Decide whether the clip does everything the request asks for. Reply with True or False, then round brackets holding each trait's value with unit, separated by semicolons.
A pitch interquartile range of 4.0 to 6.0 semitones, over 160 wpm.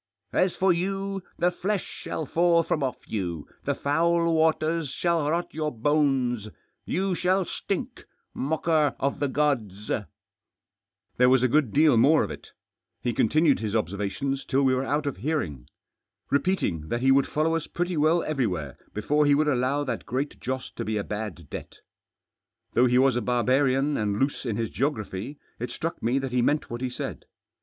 True (4.8 semitones; 185 wpm)